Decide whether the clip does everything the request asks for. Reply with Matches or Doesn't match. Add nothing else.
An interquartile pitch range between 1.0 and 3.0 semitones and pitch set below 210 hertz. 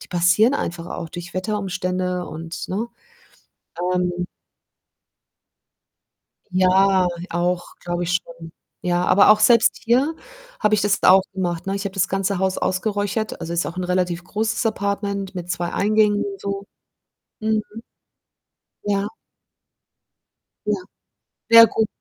Matches